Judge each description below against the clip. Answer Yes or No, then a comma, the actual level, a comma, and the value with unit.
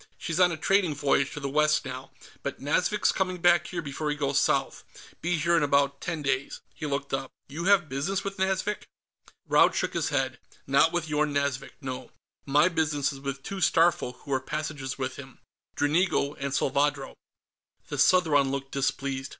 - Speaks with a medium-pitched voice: Yes, medium, 145 Hz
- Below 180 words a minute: No, average, 185 wpm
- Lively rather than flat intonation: No, average, 3.6 semitones